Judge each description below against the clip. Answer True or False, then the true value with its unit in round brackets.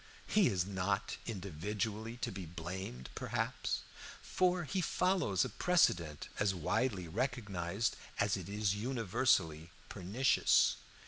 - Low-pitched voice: True (100 Hz)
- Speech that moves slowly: True (115 wpm)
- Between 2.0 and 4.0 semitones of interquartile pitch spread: False (5.3 semitones)